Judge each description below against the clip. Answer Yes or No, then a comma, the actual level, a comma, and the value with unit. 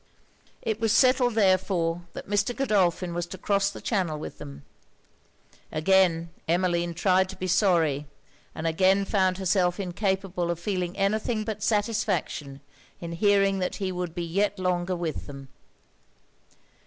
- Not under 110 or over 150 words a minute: Yes, average, 145 wpm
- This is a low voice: No, medium, 185 Hz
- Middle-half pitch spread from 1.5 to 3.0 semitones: Yes, average, 2.7 semitones